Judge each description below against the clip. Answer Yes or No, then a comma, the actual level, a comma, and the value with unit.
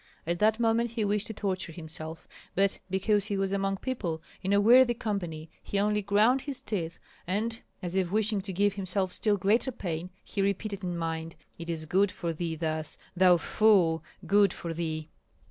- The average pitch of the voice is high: Yes, high, 195 Hz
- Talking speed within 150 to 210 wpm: Yes, average, 185 wpm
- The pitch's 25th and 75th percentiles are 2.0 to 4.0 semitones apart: Yes, average, 3.7 semitones